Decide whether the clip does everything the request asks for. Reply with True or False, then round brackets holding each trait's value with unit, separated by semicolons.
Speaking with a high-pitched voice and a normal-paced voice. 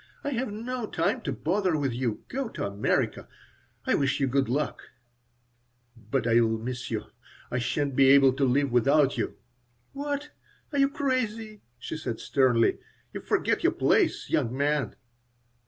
False (140 Hz; 155 wpm)